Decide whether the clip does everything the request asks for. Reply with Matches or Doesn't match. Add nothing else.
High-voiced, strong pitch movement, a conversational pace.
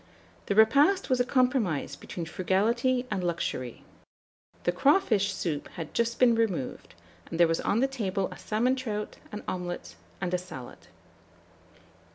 Matches